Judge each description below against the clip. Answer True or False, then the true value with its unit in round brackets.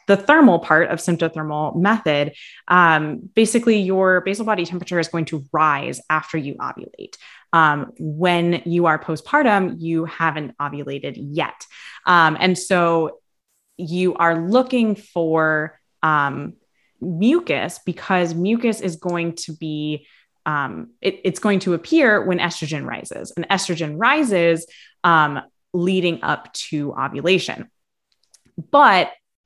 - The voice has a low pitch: False (175 Hz)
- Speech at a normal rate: False (125 wpm)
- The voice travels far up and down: False (3.1 semitones)